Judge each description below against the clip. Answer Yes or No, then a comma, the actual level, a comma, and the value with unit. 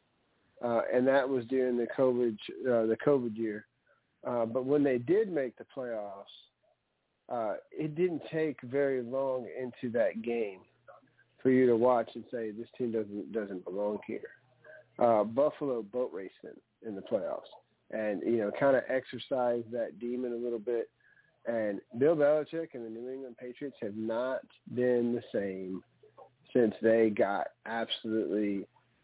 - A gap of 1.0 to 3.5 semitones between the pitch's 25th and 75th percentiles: Yes, narrow, 2.5 semitones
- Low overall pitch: Yes, low, 120 Hz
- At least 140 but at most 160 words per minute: Yes, average, 155 wpm